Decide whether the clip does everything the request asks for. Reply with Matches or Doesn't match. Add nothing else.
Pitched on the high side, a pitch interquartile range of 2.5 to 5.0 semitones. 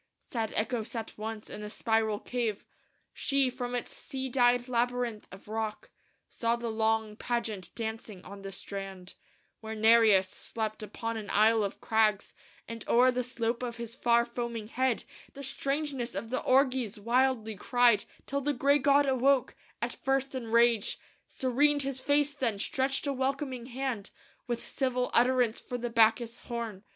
Matches